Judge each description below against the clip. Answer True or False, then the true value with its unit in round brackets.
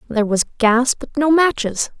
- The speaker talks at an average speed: True (180 wpm)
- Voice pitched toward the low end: False (250 Hz)